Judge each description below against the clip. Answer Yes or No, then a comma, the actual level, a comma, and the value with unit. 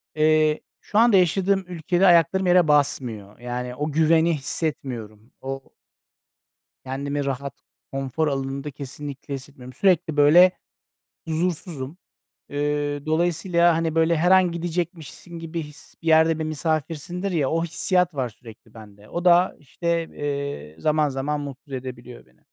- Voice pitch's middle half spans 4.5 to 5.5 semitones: No, average, 3.9 semitones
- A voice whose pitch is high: No, medium, 155 Hz